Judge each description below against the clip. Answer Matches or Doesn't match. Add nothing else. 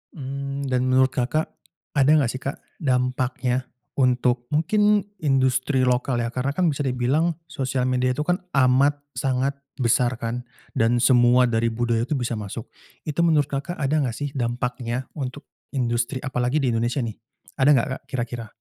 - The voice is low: Matches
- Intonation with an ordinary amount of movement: Doesn't match